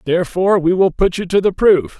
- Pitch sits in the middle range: Yes, medium, 180 Hz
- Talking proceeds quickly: Yes, fast, 240 wpm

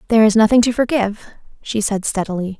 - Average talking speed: Yes, average, 185 wpm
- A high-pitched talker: Yes, high, 215 Hz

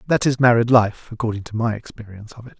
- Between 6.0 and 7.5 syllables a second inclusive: Yes, 6.7 syllables/s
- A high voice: No, low, 115 Hz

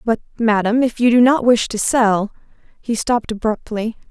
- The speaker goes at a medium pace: Yes, average, 175 wpm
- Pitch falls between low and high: No, high, 225 Hz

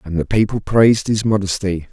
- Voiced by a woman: No, male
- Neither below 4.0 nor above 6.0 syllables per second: Yes, 5.5 syllables/s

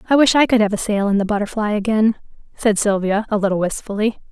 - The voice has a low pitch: No, high, 210 Hz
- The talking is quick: Yes, fast, 225 wpm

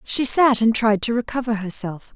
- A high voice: Yes, high, 225 Hz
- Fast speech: No, average, 195 wpm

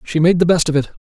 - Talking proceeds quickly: Yes, fast, 345 wpm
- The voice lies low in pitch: No, medium, 165 Hz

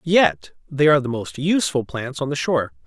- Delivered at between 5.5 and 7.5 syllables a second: Yes, 5.6 syllables/s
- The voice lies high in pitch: No, medium, 140 Hz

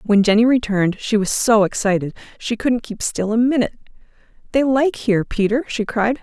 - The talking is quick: No, average, 185 wpm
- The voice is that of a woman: Yes, female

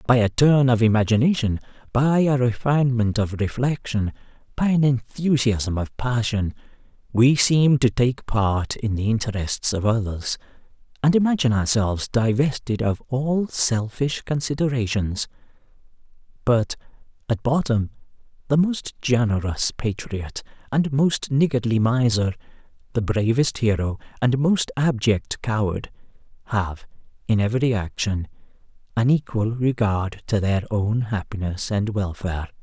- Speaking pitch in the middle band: No, low, 120 Hz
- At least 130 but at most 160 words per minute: No, slow, 120 wpm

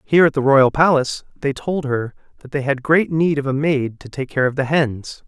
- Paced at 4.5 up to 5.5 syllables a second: Yes, 5.2 syllables/s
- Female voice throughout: No, male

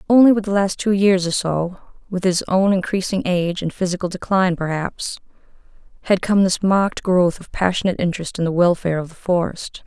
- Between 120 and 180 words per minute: Yes, average, 175 wpm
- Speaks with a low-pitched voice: No, medium, 185 Hz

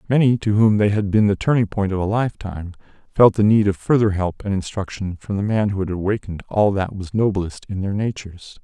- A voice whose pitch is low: Yes, low, 100 Hz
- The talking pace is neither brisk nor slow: No, fast, 230 wpm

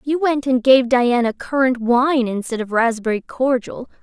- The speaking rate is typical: Yes, average, 165 wpm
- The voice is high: Yes, very high, 250 Hz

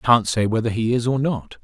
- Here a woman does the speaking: No, male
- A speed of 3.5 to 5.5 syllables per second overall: Yes, 5.1 syllables/s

